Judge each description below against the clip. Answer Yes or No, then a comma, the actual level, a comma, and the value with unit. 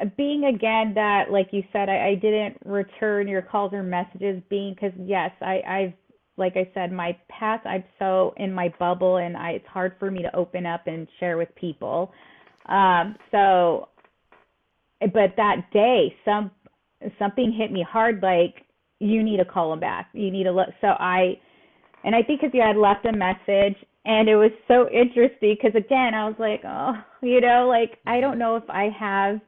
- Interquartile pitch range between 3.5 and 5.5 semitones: No, average, 3.0 semitones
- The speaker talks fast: No, average, 190 wpm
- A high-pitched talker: Yes, high, 200 Hz